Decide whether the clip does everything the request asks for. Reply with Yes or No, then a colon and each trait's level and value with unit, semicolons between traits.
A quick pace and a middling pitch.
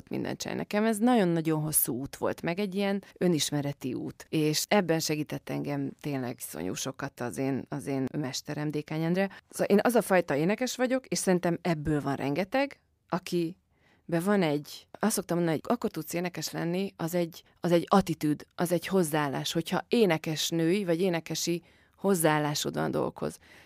Yes: fast, 160 wpm; medium, 165 Hz